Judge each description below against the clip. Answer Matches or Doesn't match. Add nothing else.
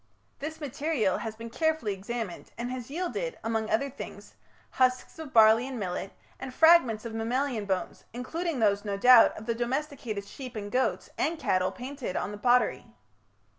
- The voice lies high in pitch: Matches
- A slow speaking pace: Doesn't match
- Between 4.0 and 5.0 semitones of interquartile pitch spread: Matches